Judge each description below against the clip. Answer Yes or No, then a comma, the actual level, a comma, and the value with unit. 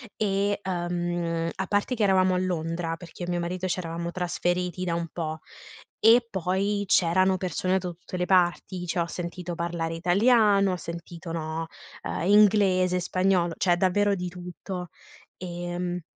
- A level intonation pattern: Yes, narrow, 1.7 semitones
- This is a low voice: No, medium, 180 Hz